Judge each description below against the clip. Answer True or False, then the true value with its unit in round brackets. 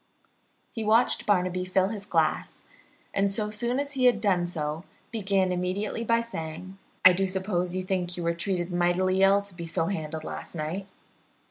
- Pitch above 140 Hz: True (185 Hz)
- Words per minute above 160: True (175 wpm)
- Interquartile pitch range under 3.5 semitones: True (2.7 semitones)